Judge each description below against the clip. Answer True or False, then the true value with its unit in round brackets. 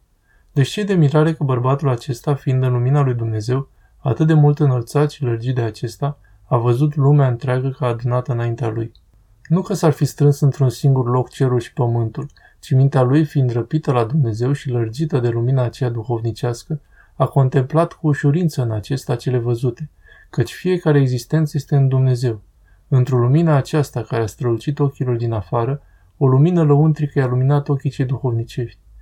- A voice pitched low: True (130 Hz)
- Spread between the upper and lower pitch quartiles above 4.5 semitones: False (3.3 semitones)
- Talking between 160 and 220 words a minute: True (170 wpm)